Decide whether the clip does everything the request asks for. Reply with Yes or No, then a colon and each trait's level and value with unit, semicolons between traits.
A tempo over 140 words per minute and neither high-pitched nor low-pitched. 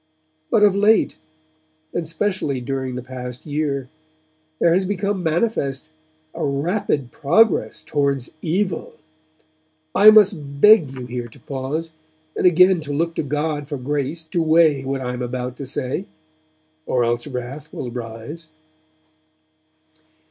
No: slow, 135 wpm; medium, 145 Hz